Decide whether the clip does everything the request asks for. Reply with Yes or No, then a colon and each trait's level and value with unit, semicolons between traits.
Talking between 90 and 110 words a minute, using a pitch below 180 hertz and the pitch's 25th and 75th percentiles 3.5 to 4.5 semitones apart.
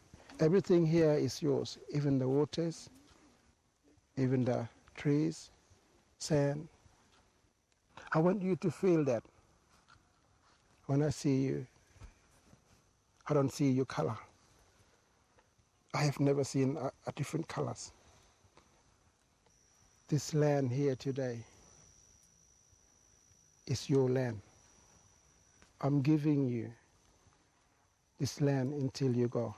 No: average, 100 wpm; low, 135 Hz; average, 5.2 semitones